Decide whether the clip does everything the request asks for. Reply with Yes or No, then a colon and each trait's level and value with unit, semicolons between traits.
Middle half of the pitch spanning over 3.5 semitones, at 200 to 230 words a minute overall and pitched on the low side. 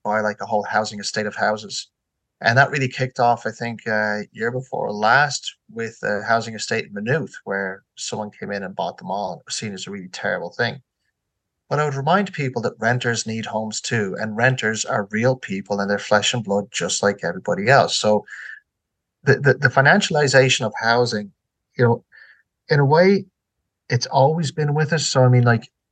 Yes: average, 4.1 semitones; fast, 205 wpm; low, 115 Hz